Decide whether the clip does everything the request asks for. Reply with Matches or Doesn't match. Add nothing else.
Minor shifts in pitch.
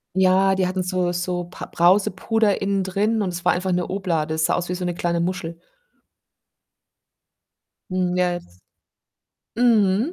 Matches